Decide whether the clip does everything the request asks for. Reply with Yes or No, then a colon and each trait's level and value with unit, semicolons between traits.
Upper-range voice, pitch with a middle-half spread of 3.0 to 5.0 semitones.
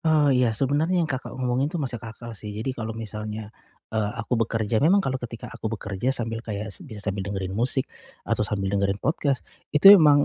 No: low, 115 Hz; average, 4.6 semitones